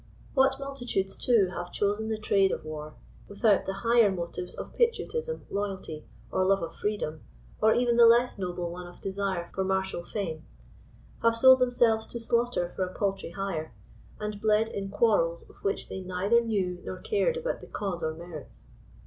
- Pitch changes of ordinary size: Yes, average, 4.3 semitones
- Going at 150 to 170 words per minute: No, average, 180 wpm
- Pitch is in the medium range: No, high, 200 Hz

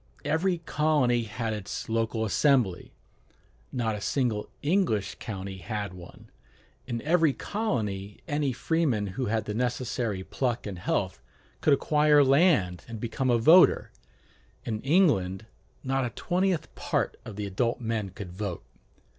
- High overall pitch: No, low, 115 Hz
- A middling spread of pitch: No, wide, 6.0 semitones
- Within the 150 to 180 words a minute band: No, average, 140 wpm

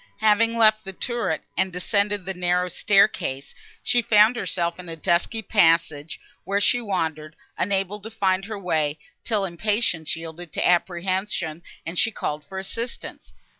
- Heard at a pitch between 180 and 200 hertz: Yes, high, 190 Hz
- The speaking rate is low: No, average, 150 wpm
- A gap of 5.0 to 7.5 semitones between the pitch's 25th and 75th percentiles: No, average, 3.8 semitones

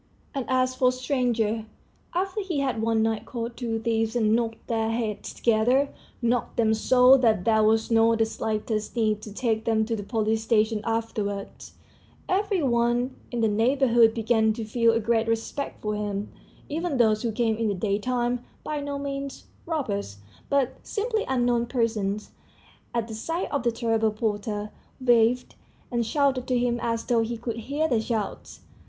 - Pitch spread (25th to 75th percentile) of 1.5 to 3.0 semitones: Yes, narrow, 2.4 semitones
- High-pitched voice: Yes, high, 230 Hz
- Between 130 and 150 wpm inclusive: No, average, 170 wpm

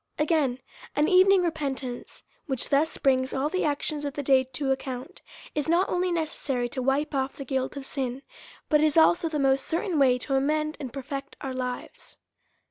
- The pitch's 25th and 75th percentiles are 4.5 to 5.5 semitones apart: No, average, 2.7 semitones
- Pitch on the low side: No, very high, 280 Hz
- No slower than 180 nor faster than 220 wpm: Yes, average, 195 wpm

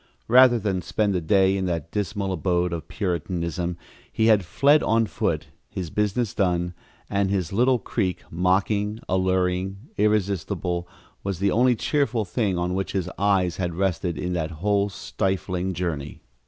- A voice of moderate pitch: No, very low, 95 Hz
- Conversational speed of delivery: Yes, average, 155 wpm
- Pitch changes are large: No, average, 2.7 semitones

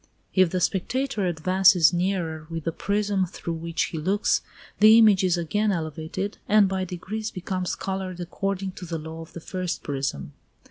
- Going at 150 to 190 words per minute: Yes, average, 170 wpm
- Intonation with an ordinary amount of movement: Yes, average, 3.0 semitones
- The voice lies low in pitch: No, medium, 185 Hz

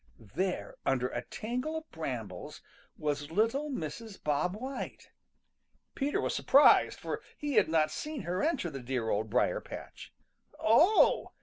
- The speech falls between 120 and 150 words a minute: Yes, average, 140 wpm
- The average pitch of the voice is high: No, medium, 180 Hz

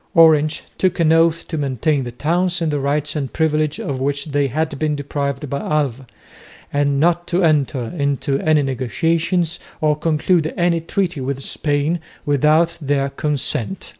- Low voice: No, medium, 150 Hz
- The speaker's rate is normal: Yes, average, 160 wpm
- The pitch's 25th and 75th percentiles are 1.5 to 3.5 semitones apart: Yes, narrow, 2.6 semitones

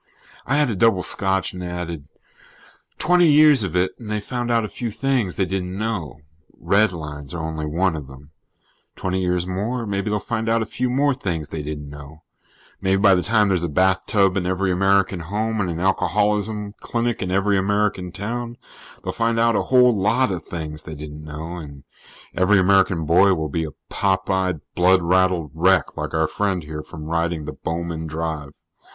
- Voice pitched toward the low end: Yes, very low, 95 Hz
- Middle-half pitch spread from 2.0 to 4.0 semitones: No, average, 4.5 semitones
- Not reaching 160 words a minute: No, average, 190 wpm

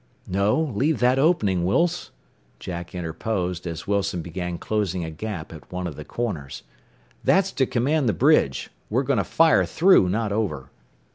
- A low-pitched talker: Yes, low, 100 Hz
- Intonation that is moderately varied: No, wide, 7.0 semitones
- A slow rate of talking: No, average, 160 wpm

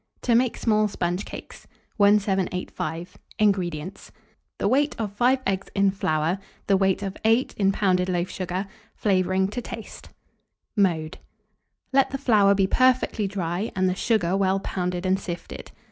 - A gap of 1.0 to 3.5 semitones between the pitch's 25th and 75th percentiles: Yes, narrow, 2.6 semitones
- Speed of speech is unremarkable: Yes, average, 145 wpm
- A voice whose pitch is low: No, high, 195 Hz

